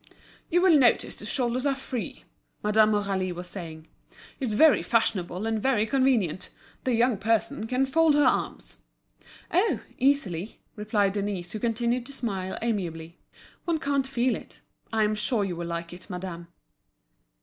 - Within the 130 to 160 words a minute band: Yes, average, 155 wpm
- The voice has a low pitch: No, high, 220 Hz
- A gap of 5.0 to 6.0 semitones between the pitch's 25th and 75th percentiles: Yes, wide, 5.6 semitones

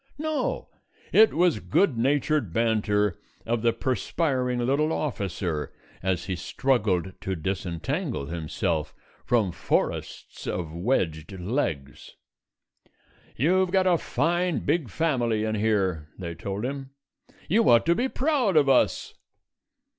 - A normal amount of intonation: No, wide, 8.7 semitones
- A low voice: Yes, low, 115 Hz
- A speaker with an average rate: No, slow, 120 wpm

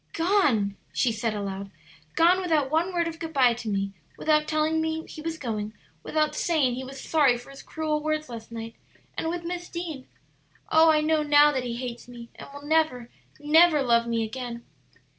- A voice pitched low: No, very high, 295 Hz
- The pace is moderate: Yes, average, 195 wpm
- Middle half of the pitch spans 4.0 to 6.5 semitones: Yes, average, 5.2 semitones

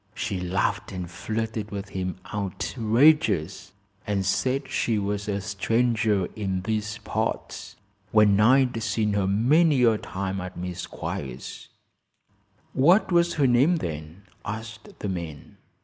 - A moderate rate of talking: No, slow, 130 wpm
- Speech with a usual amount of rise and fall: Yes, average, 3.6 semitones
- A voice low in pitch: Yes, low, 105 Hz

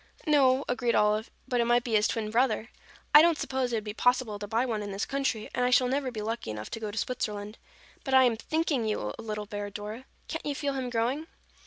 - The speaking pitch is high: Yes, high, 235 Hz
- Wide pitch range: No, average, 3.6 semitones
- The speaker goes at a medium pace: No, fast, 245 wpm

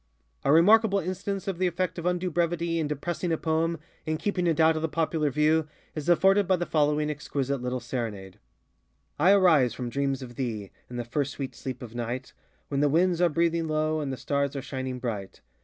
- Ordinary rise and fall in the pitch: Yes, average, 4.5 semitones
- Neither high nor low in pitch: Yes, medium, 155 Hz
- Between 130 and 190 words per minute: No, fast, 205 wpm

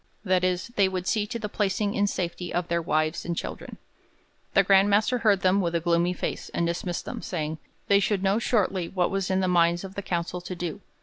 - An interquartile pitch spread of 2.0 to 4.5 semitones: Yes, narrow, 2.5 semitones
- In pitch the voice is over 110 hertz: Yes, medium, 185 Hz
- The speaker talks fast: Yes, fast, 230 wpm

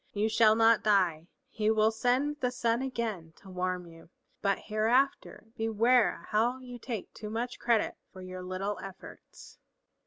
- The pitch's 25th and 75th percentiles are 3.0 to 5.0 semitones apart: Yes, average, 3.7 semitones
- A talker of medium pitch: No, high, 220 Hz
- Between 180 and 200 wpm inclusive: No, average, 155 wpm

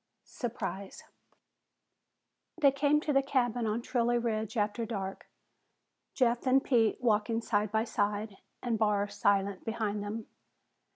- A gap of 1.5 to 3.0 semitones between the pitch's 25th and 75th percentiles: Yes, average, 2.7 semitones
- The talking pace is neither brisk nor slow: No, slow, 125 wpm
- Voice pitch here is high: Yes, high, 225 Hz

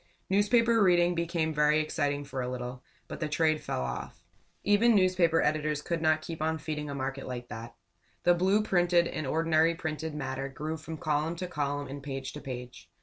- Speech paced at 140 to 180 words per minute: No, average, 190 wpm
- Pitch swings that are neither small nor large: Yes, average, 3.4 semitones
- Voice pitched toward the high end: No, medium, 155 Hz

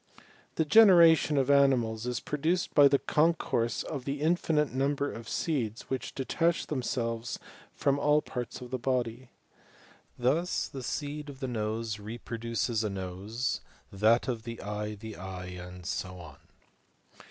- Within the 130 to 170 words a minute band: Yes, average, 150 wpm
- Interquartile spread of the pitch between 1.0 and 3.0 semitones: No, average, 4.5 semitones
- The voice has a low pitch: Yes, low, 125 Hz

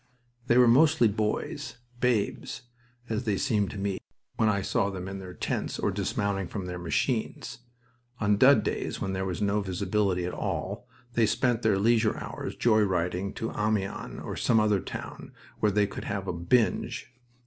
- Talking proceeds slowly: No, average, 175 wpm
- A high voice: No, low, 105 Hz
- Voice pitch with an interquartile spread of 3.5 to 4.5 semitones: No, average, 2.7 semitones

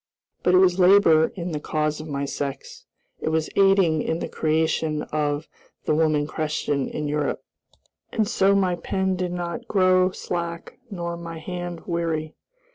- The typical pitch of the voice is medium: Yes, medium, 170 Hz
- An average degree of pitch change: Yes, average, 3.0 semitones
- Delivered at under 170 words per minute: Yes, average, 160 wpm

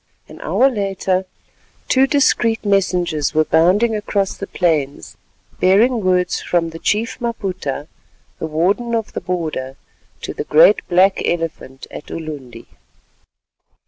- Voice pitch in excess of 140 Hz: Yes, medium, 185 Hz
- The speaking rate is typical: No, slow, 125 wpm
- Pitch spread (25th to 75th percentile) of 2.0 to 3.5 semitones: No, average, 5.0 semitones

